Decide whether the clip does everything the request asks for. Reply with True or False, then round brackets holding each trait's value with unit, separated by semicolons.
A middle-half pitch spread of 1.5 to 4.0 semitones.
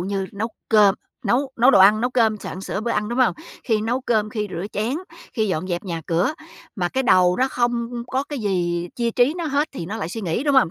False (4.5 semitones)